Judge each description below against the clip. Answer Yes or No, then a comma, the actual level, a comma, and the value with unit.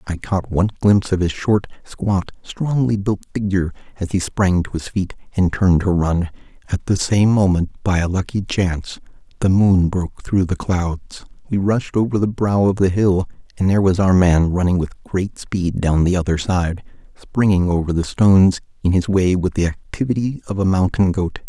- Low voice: Yes, very low, 95 Hz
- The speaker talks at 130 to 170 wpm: No, average, 195 wpm